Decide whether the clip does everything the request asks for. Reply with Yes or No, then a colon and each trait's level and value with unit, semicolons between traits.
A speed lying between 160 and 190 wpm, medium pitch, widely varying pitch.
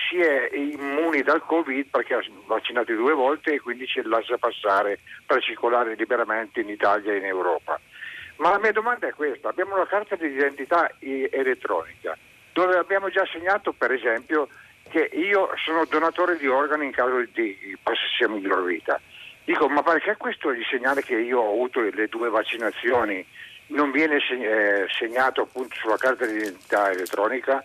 Yes: average, 165 wpm; medium, 150 Hz; wide, 6.7 semitones